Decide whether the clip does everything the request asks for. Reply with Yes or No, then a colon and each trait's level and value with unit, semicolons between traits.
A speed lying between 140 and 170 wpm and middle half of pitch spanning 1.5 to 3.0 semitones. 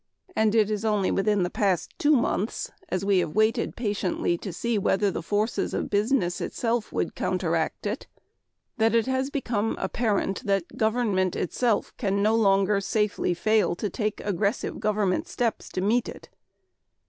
Yes: average, 160 wpm; narrow, 2.6 semitones